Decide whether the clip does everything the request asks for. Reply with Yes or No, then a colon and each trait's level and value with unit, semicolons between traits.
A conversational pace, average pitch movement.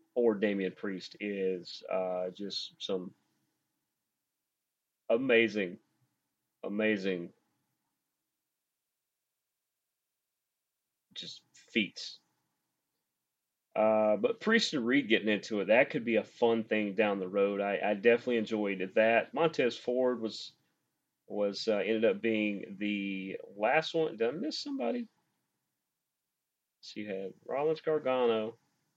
No: slow, 110 wpm; average, 4.0 semitones